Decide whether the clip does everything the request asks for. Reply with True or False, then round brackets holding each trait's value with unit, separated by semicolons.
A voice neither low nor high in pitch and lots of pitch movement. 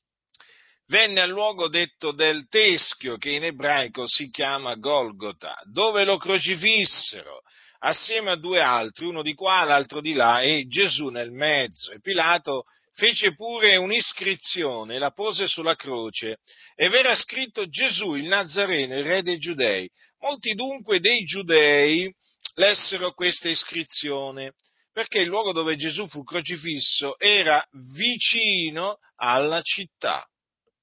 True (175 Hz; 6.1 semitones)